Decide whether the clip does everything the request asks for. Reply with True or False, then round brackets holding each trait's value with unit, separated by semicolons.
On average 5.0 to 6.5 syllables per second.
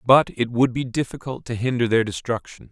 True (5.5 syllables/s)